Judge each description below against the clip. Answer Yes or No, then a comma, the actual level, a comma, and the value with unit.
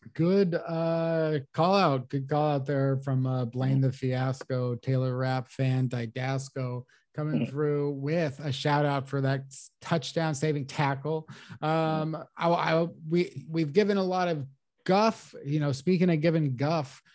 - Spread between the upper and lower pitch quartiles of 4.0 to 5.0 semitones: No, average, 3.6 semitones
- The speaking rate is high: No, average, 145 wpm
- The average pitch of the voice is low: No, medium, 145 Hz